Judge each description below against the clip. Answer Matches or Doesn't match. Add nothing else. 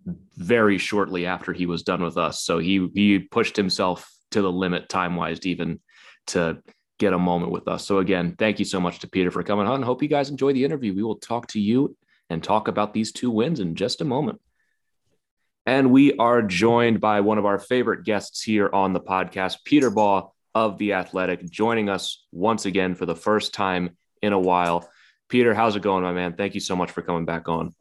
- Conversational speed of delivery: Doesn't match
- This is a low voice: Matches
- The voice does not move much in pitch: Doesn't match